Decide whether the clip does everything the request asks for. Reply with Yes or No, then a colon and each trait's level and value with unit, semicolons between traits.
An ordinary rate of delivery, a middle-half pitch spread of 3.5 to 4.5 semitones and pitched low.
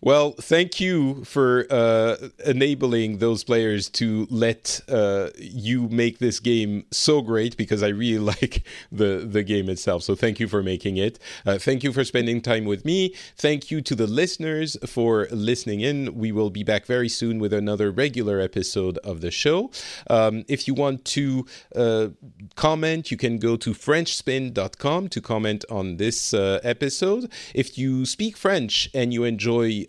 Yes: average, 170 wpm; average, 4.2 semitones; low, 115 Hz